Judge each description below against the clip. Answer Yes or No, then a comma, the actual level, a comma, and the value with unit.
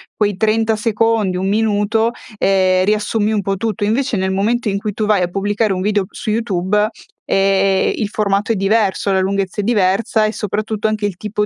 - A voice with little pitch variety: Yes, narrow, 1.9 semitones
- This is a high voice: Yes, high, 205 Hz